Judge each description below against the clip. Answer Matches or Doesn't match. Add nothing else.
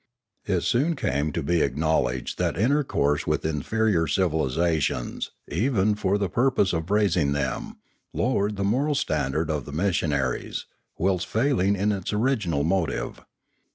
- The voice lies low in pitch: Matches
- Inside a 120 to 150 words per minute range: Matches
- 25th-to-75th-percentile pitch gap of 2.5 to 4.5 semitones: Doesn't match